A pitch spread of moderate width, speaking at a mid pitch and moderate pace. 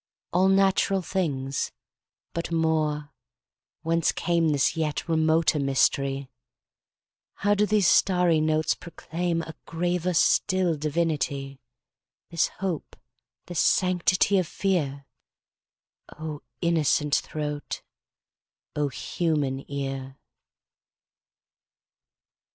No: average, 3.4 semitones; medium, 160 Hz; slow, 70 wpm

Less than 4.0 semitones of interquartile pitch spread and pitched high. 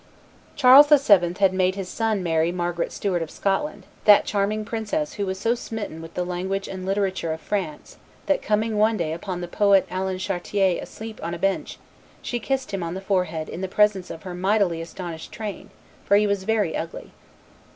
Yes: average, 3.2 semitones; high, 195 Hz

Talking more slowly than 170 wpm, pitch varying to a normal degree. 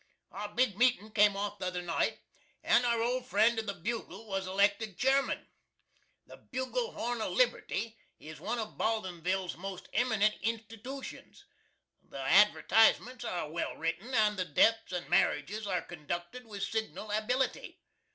Yes: average, 150 wpm; average, 3.9 semitones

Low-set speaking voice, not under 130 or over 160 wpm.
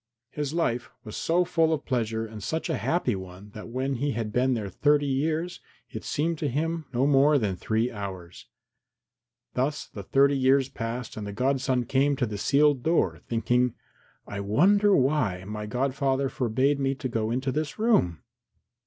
No: low, 130 Hz; average, 175 wpm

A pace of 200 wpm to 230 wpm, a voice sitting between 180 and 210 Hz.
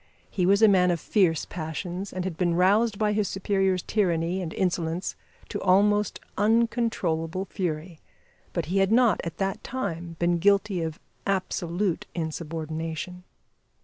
No: average, 145 wpm; medium, 185 Hz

